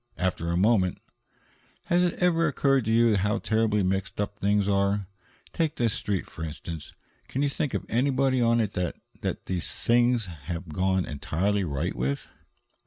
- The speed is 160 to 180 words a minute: Yes, average, 165 wpm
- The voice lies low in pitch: Yes, low, 105 Hz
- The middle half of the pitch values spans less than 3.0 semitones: No, average, 4.7 semitones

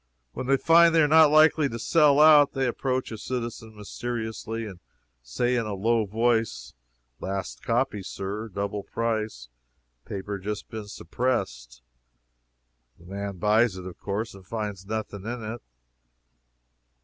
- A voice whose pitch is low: Yes, low, 110 Hz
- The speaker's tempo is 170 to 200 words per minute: No, average, 145 wpm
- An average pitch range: Yes, average, 3.5 semitones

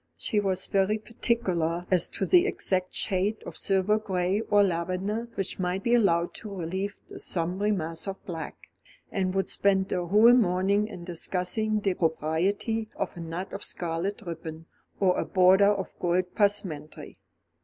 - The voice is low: No, high, 190 Hz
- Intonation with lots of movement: No, average, 2.7 semitones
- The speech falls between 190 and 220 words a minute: No, average, 160 wpm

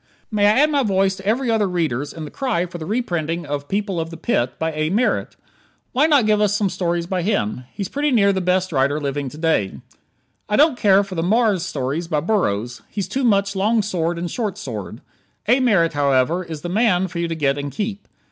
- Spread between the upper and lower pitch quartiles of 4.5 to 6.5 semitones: Yes, average, 5.2 semitones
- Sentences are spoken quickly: Yes, fast, 225 wpm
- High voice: No, medium, 180 Hz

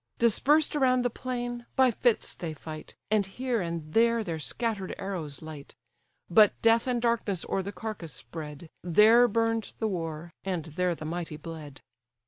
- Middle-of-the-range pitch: No, high, 195 Hz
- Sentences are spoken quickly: No, average, 160 wpm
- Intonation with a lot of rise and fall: Yes, wide, 6.2 semitones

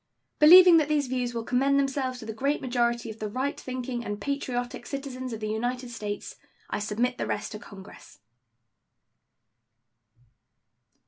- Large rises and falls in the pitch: No, average, 3.4 semitones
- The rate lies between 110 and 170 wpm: Yes, average, 150 wpm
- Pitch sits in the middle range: No, very high, 250 Hz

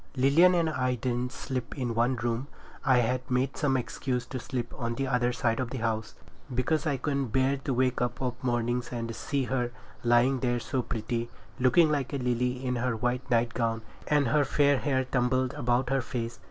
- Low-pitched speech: Yes, low, 125 Hz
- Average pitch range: No, narrow, 1.8 semitones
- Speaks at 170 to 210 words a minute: Yes, fast, 205 wpm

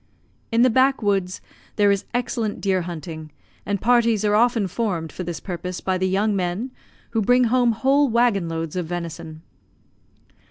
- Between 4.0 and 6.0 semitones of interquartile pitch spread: Yes, average, 4.9 semitones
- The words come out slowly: No, average, 165 wpm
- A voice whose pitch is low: No, high, 200 Hz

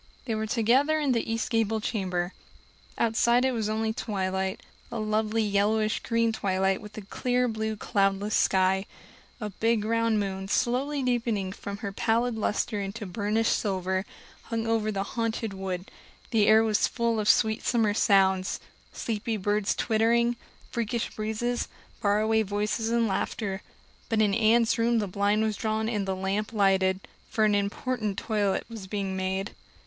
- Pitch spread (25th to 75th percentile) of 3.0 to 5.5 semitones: No, narrow, 2.4 semitones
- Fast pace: No, average, 155 wpm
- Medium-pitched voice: No, high, 215 Hz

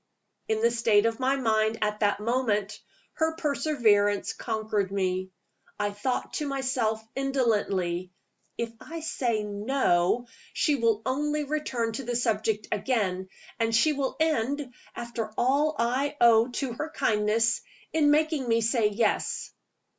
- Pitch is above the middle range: Yes, high, 230 Hz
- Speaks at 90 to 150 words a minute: Yes, average, 140 wpm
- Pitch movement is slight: No, average, 4.2 semitones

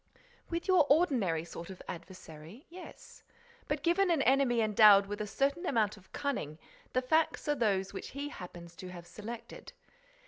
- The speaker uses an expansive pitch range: Yes, wide, 7.6 semitones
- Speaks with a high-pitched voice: Yes, high, 220 Hz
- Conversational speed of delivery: Yes, average, 165 wpm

